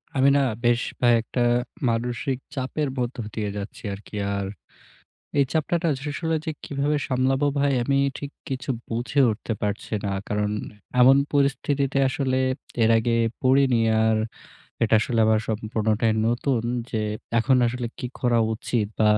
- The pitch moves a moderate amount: Yes, average, 3.6 semitones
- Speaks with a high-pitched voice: No, low, 125 Hz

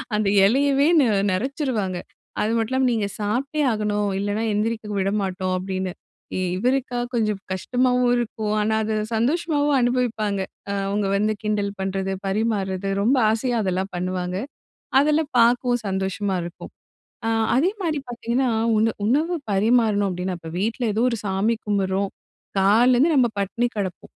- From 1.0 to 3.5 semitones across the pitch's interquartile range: No, average, 4.1 semitones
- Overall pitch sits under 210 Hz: No, high, 215 Hz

